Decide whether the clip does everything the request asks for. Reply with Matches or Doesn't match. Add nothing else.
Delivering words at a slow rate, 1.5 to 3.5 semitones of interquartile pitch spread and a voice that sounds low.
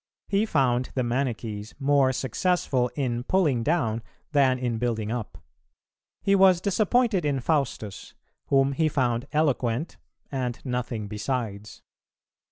Doesn't match